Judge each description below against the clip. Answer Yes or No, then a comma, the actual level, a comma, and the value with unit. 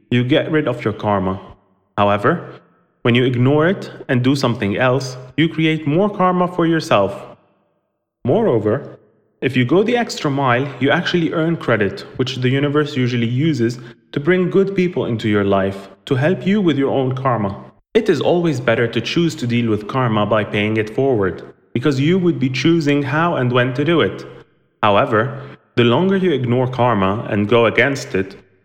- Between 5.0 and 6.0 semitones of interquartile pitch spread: Yes, wide, 5.4 semitones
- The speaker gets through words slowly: No, average, 180 wpm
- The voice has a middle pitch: No, low, 130 Hz